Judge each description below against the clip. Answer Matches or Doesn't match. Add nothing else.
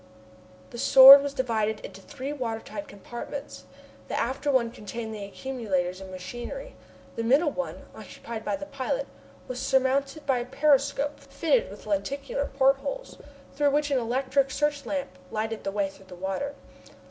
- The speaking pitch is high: Matches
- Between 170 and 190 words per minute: Doesn't match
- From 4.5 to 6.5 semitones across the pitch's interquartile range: Doesn't match